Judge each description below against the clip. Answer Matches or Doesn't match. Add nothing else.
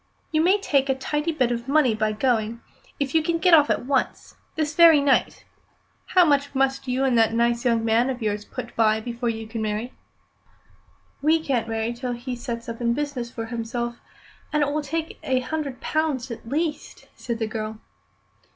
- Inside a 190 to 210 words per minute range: Matches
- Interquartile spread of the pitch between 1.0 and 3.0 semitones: Doesn't match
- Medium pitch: Doesn't match